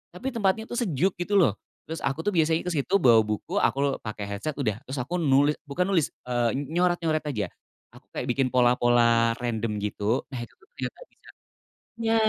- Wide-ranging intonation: Yes, wide, 6.8 semitones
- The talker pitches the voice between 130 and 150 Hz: Yes, medium, 140 Hz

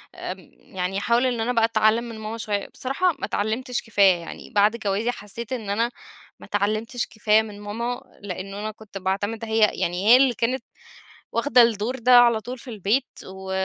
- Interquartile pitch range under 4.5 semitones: Yes, average, 2.8 semitones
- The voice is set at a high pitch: Yes, high, 220 Hz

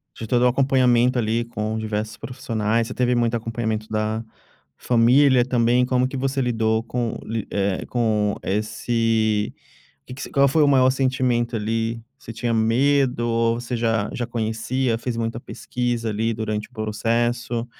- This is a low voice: Yes, low, 115 Hz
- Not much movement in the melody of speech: Yes, narrow, 2.1 semitones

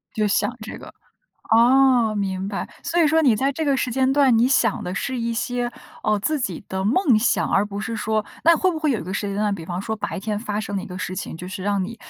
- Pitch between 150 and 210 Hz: No, high, 220 Hz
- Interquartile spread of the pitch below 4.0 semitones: No, average, 4.7 semitones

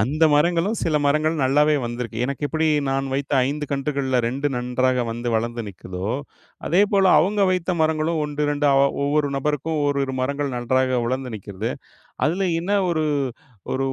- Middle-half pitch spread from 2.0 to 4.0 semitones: Yes, average, 3.5 semitones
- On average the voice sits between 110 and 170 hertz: Yes, medium, 140 Hz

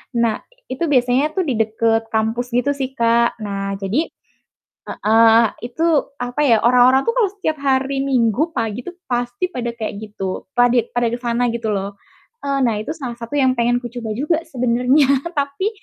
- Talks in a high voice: Yes, high, 245 Hz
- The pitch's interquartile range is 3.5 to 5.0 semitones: No, average, 3.0 semitones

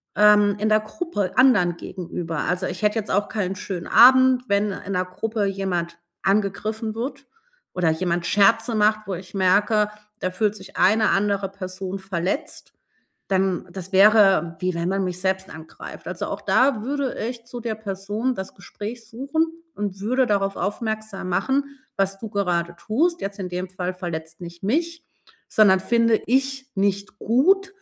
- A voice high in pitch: Yes, high, 200 Hz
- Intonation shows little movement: No, average, 3.4 semitones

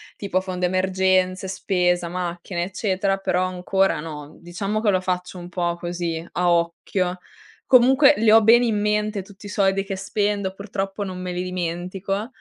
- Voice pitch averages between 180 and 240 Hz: Yes, medium, 185 Hz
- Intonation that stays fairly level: Yes, narrow, 2.1 semitones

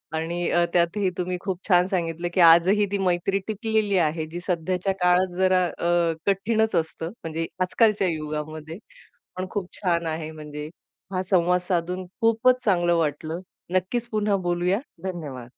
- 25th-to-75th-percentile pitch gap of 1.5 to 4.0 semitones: Yes, average, 2.9 semitones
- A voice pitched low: No, medium, 180 Hz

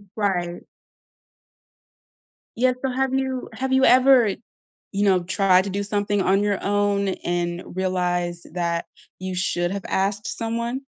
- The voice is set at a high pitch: Yes, high, 200 Hz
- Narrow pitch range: No, average, 4.2 semitones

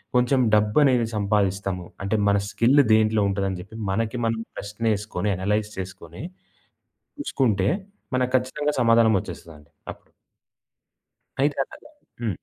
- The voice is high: No, low, 105 Hz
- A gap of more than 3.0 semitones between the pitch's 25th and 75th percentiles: Yes, average, 3.4 semitones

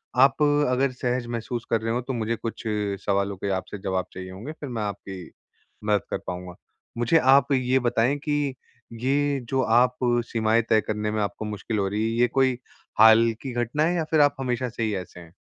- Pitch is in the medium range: No, low, 115 Hz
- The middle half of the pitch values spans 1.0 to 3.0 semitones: No, average, 3.8 semitones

